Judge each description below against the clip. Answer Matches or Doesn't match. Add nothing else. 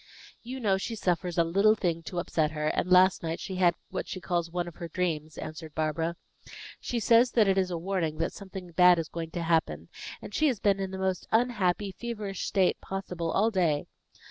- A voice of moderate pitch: Matches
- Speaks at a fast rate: Matches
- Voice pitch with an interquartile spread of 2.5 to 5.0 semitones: Matches